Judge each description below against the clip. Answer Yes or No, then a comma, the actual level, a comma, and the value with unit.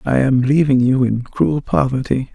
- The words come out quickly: No, average, 180 wpm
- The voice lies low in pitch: Yes, low, 130 Hz